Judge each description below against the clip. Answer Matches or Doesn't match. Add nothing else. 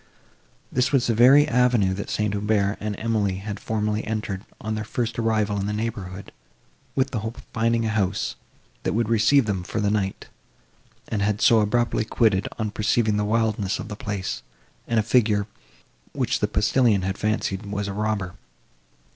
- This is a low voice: Matches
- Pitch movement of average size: Doesn't match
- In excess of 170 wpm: Matches